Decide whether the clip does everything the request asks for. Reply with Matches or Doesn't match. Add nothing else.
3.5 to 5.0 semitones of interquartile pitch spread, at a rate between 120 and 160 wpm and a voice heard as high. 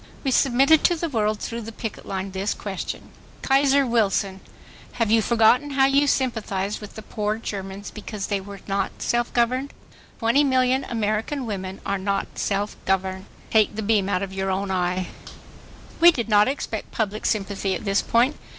Doesn't match